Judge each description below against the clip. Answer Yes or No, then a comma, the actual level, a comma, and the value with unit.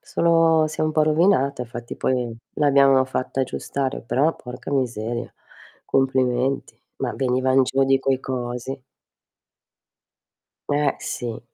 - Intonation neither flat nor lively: No, narrow, 2.3 semitones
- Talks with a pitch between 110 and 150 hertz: Yes, low, 135 Hz